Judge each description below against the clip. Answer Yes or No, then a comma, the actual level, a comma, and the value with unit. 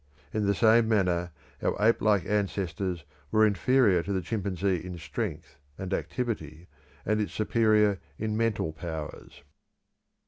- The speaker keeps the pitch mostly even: No, average, 3.4 semitones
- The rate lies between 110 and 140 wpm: Yes, slow, 135 wpm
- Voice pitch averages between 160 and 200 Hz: No, low, 100 Hz